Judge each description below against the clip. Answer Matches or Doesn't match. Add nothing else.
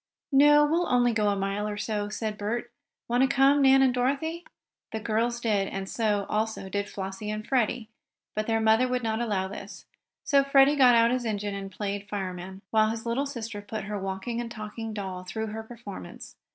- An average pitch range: Matches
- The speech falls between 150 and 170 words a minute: Doesn't match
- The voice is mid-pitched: Doesn't match